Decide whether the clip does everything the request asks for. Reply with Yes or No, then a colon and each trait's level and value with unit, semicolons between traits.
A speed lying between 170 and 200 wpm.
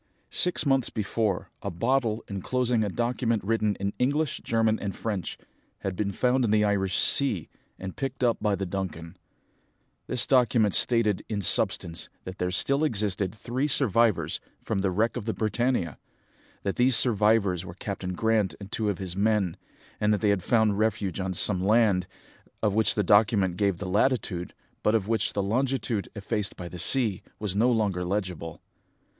Yes: average, 175 wpm